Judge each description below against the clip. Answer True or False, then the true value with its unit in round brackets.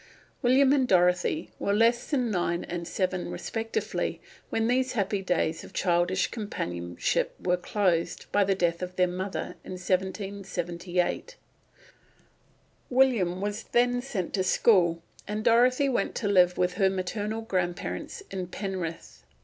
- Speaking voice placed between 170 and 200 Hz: True (190 Hz)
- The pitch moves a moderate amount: True (3.9 semitones)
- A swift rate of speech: False (135 wpm)